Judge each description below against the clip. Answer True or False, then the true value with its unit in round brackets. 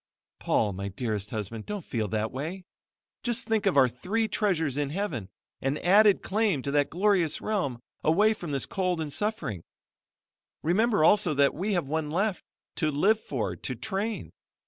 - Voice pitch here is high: False (160 Hz)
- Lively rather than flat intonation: True (7.5 semitones)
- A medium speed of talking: True (170 wpm)